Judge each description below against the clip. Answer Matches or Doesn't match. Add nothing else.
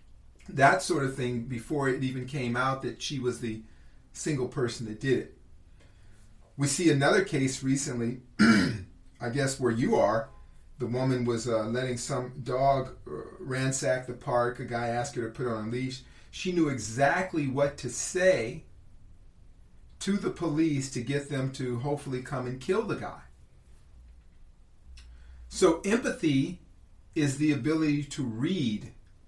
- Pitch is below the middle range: Matches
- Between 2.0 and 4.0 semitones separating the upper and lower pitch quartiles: Matches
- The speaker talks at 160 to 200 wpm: Doesn't match